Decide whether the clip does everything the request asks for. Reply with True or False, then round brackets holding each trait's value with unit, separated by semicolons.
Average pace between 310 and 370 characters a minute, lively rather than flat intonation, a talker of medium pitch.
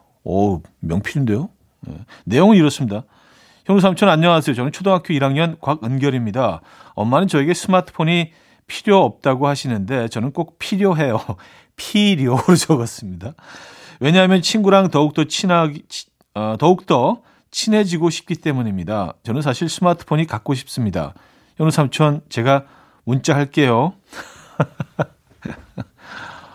False (290 characters per minute; 5.7 semitones; 150 Hz)